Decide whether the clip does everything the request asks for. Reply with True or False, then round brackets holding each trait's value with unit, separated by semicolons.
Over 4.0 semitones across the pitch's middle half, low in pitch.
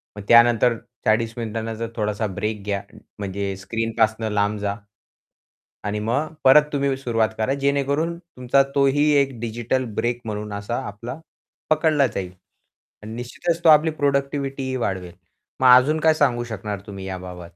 True (4.7 semitones; 115 Hz)